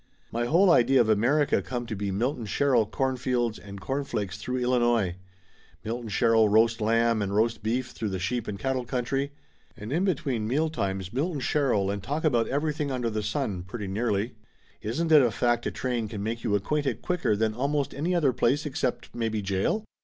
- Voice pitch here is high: No, low, 120 Hz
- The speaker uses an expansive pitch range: No, average, 4.1 semitones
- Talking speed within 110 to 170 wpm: No, average, 190 wpm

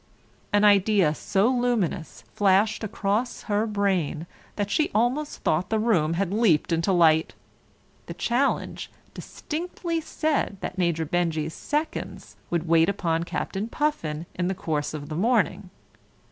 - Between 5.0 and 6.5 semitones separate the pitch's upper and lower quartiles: Yes, wide, 5.4 semitones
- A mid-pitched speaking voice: No, high, 195 Hz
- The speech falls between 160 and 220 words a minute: No, slow, 135 wpm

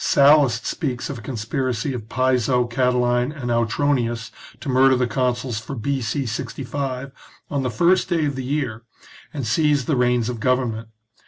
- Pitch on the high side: No, low, 125 Hz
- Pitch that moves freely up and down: No, narrow, 2.6 semitones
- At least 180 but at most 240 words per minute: No, average, 160 wpm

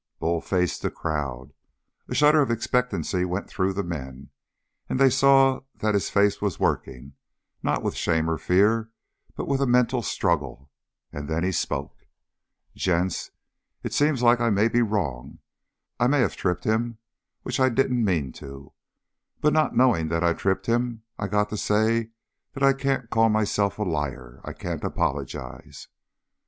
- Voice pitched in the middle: No, low, 105 Hz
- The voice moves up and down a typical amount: No, wide, 6.8 semitones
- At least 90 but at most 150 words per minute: No, average, 165 wpm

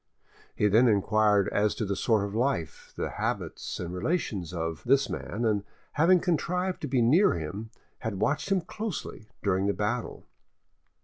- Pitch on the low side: Yes, low, 110 Hz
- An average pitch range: No, wide, 6.3 semitones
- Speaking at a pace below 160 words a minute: No, average, 165 wpm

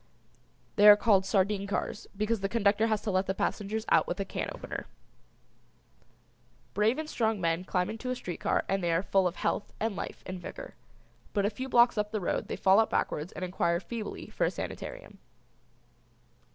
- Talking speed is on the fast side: No, average, 195 wpm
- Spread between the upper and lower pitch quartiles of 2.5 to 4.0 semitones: Yes, average, 2.8 semitones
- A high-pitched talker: Yes, high, 205 Hz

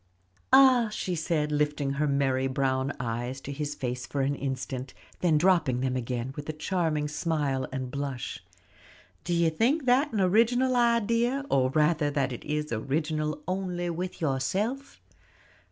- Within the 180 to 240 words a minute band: No, average, 155 wpm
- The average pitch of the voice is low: No, medium, 150 Hz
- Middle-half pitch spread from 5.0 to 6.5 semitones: Yes, wide, 5.6 semitones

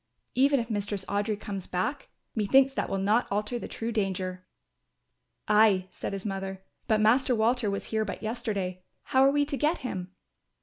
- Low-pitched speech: No, high, 215 Hz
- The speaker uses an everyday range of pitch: Yes, average, 4.0 semitones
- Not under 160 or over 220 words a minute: Yes, average, 175 wpm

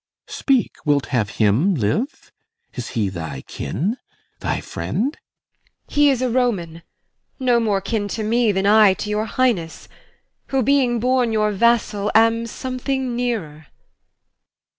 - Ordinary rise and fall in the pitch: No, wide, 7.0 semitones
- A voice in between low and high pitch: No, high, 215 Hz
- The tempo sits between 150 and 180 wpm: No, average, 140 wpm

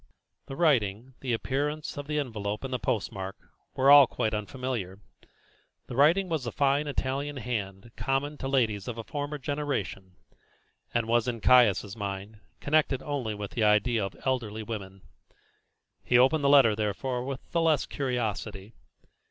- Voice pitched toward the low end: Yes, low, 125 Hz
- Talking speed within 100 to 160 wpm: Yes, average, 155 wpm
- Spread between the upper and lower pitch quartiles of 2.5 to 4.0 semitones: No, average, 4.9 semitones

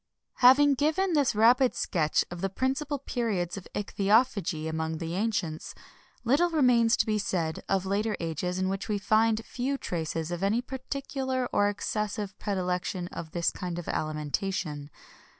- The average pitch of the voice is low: No, high, 205 Hz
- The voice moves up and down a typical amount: No, wide, 6.1 semitones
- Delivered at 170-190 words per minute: No, average, 160 wpm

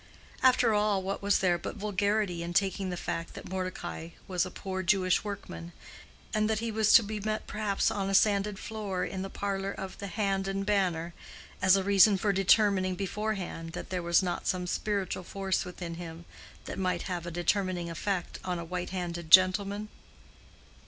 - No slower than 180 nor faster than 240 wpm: Yes, average, 185 wpm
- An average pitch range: No, narrow, 2.2 semitones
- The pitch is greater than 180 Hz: Yes, high, 190 Hz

